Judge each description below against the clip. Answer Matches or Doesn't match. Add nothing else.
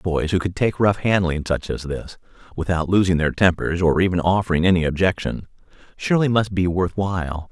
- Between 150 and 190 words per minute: Matches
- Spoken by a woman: Doesn't match